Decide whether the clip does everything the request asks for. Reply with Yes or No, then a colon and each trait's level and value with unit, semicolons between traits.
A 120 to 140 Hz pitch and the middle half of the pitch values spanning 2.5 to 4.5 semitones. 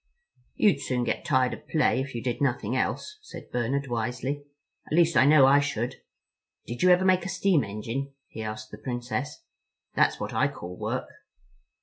Yes: low, 135 Hz; average, 4.0 semitones